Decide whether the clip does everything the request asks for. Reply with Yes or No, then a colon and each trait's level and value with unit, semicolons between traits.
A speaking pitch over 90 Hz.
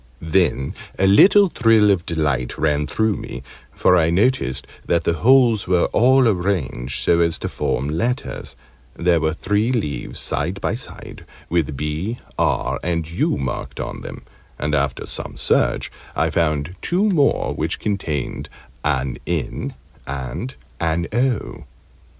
No: very low, 85 Hz